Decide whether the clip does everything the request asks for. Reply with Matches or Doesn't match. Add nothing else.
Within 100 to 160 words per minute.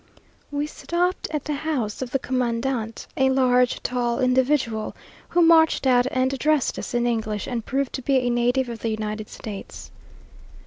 Doesn't match